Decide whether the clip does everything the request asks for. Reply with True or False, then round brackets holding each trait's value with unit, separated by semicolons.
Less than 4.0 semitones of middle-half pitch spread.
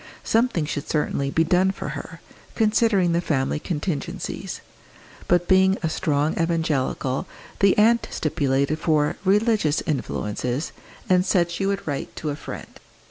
False (4.5 semitones)